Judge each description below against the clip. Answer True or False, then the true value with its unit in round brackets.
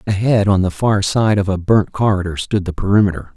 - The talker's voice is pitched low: True (100 Hz)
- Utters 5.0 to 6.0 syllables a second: True (5.6 syllables/s)